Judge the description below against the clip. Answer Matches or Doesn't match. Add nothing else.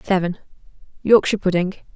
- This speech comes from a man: Doesn't match